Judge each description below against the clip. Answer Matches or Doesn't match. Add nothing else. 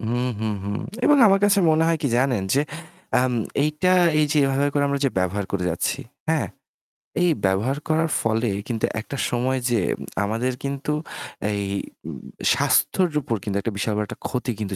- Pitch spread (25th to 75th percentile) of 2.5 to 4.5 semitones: Doesn't match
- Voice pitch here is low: Matches